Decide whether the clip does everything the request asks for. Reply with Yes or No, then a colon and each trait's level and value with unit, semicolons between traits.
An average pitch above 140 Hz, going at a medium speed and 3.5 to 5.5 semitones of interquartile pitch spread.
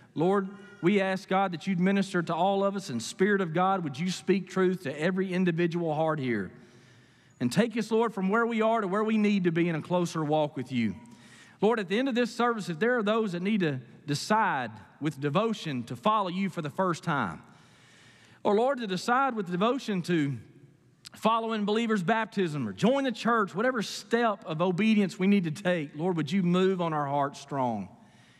No: high, 190 Hz; fast, 210 wpm; average, 5.1 semitones